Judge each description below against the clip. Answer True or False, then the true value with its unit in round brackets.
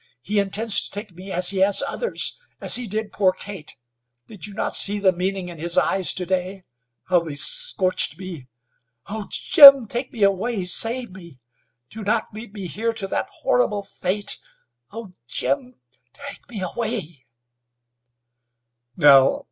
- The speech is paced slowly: False (155 wpm)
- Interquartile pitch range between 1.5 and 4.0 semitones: True (3.3 semitones)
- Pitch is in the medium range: False (195 Hz)